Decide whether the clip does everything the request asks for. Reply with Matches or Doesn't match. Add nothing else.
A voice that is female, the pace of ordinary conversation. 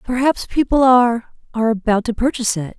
Matches